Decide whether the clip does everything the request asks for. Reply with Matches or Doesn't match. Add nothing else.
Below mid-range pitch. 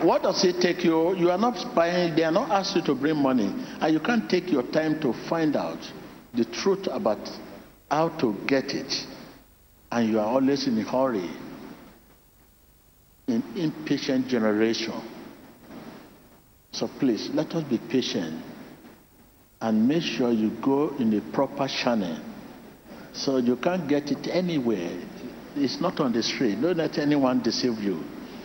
Doesn't match